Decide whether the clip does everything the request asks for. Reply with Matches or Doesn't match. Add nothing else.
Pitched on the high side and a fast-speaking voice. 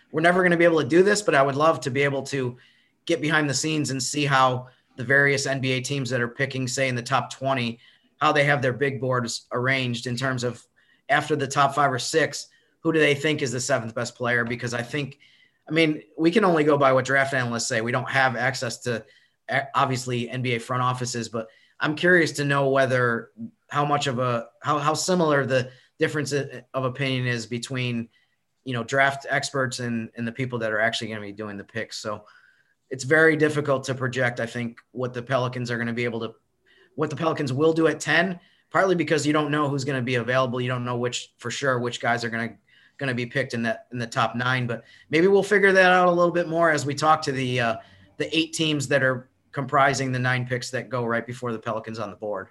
Doesn't match